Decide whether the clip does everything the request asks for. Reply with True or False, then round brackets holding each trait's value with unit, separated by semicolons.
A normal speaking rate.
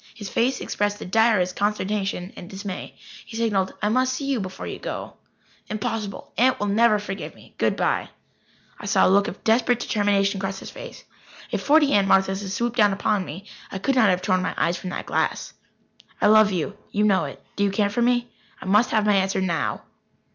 False (210 wpm)